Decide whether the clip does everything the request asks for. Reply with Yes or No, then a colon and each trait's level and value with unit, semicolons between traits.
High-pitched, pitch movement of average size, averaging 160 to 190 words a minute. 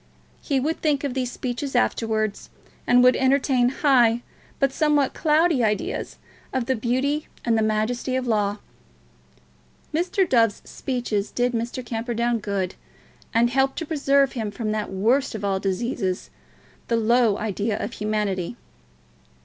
No: high, 240 Hz; average, 3.8 semitones; average, 140 wpm